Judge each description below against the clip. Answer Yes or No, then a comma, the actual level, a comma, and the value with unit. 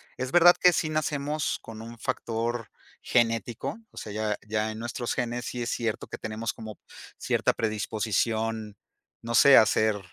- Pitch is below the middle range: Yes, low, 115 Hz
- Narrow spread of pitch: Yes, narrow, 1.9 semitones